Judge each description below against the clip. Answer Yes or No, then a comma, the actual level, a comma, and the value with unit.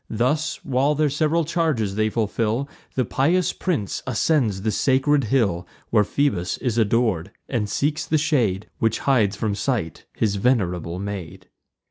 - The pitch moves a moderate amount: No, wide, 5.9 semitones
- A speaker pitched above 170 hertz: No, low, 115 Hz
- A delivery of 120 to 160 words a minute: Yes, average, 145 wpm